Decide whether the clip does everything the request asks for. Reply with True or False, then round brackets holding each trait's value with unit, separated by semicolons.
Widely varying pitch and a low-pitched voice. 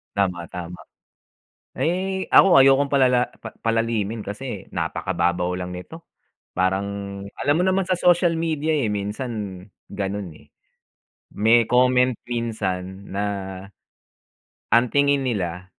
True (6.2 semitones; 115 Hz)